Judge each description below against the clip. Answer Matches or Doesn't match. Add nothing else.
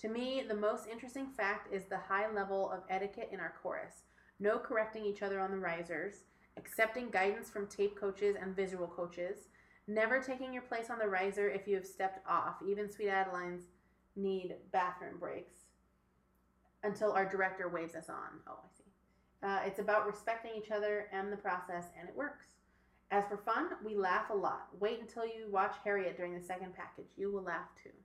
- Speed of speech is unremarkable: Matches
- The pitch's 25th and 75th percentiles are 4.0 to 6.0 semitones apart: Doesn't match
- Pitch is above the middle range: Matches